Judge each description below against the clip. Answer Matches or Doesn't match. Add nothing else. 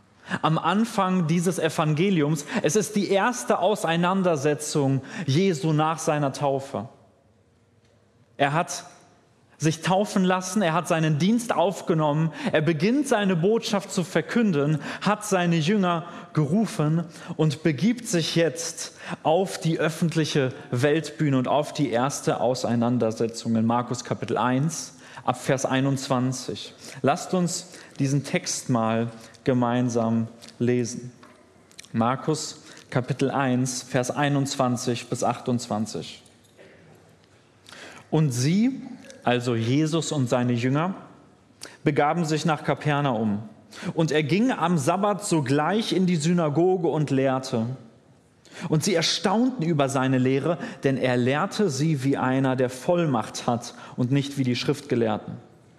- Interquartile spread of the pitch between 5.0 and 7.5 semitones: Matches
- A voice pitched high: Doesn't match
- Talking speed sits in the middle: Doesn't match